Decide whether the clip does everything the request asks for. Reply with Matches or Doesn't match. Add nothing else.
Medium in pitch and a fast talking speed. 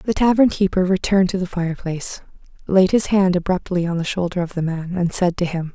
Matches